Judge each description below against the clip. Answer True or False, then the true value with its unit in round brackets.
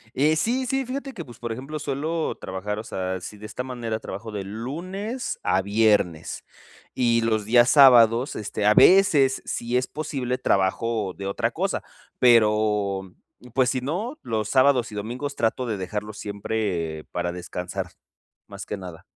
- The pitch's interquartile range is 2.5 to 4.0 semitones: False (5.1 semitones)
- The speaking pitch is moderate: False (115 Hz)